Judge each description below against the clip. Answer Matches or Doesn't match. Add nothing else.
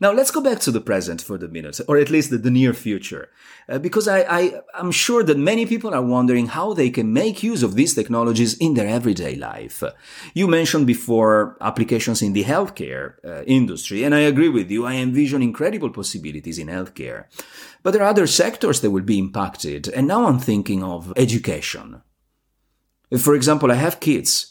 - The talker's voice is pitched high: Doesn't match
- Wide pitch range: Matches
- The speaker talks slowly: Doesn't match